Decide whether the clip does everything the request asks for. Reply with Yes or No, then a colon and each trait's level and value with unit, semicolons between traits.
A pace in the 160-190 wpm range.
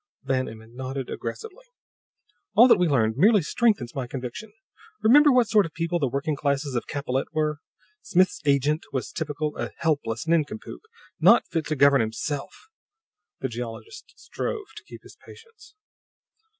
No: average, 150 wpm